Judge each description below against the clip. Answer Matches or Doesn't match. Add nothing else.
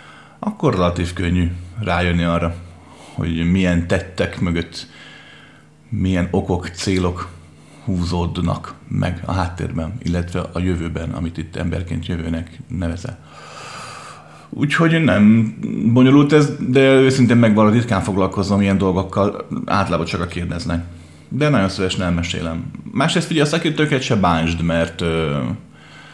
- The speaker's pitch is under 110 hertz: Matches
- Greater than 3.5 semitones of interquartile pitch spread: Matches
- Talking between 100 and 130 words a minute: Matches